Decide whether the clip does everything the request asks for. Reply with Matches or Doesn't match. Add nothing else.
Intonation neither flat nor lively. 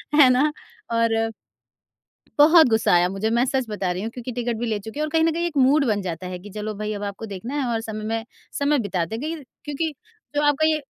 Doesn't match